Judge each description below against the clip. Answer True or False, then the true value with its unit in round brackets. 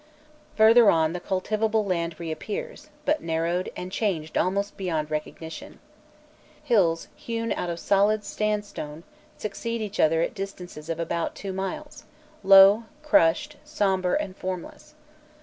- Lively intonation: False (4.2 semitones)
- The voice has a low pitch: False (190 Hz)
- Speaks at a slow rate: True (130 wpm)